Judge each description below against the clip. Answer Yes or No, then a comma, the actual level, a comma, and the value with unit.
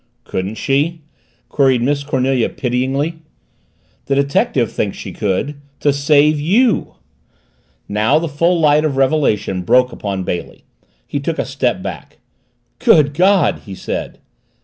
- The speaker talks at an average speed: No, slow, 130 wpm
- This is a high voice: No, medium, 140 Hz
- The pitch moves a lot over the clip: No, average, 3.9 semitones